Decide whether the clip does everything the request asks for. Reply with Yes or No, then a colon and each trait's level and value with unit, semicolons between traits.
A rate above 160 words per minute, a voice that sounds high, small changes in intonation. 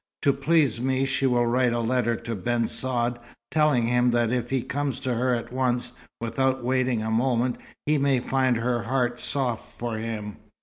No: average, 185 wpm; low, 125 Hz; narrow, 2.0 semitones